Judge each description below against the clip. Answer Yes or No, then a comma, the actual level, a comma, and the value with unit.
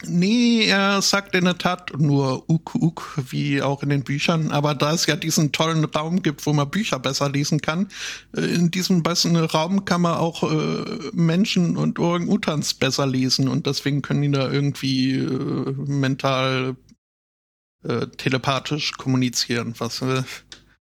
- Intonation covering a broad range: No, average, 4.3 semitones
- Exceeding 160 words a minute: No, average, 155 wpm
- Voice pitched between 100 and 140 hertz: No, medium, 150 Hz